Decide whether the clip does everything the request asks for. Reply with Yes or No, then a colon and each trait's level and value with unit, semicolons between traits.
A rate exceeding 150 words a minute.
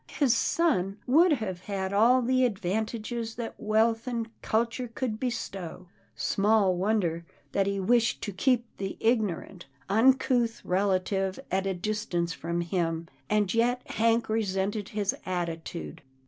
No: slow, 135 wpm